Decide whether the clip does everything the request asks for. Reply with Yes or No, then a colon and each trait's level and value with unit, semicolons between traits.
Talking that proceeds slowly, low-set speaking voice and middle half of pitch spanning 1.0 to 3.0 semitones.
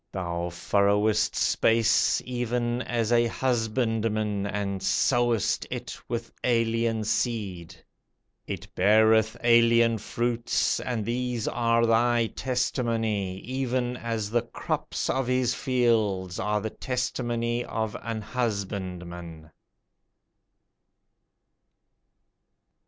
Yes: slow, 90 wpm; low, 115 Hz; narrow, 2.6 semitones